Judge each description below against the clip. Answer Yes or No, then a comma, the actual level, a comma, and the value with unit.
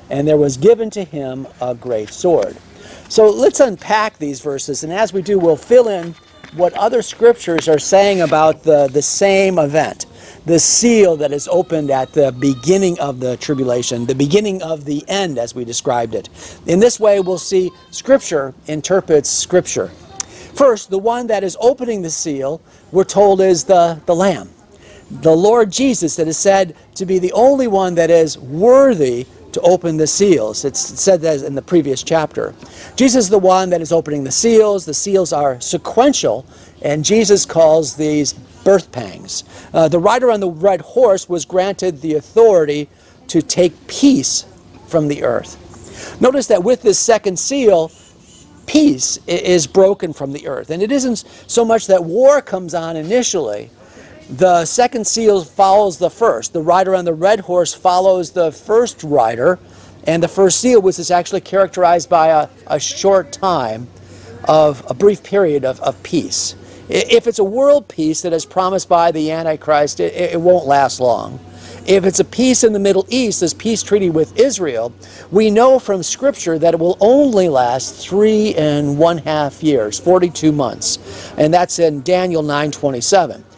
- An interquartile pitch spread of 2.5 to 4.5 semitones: No, average, 5.2 semitones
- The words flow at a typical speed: Yes, average, 175 wpm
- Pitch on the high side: No, medium, 175 Hz